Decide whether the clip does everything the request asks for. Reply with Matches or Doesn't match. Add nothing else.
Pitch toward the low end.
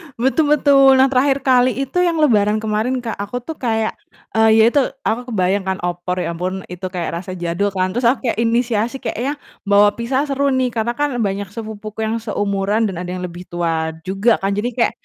Doesn't match